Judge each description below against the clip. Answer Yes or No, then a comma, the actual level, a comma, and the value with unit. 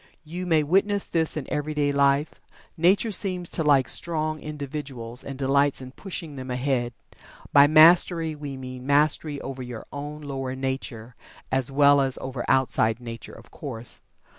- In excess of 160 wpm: No, average, 155 wpm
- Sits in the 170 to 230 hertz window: No, medium, 140 Hz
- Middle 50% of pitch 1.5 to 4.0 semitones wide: Yes, average, 2.9 semitones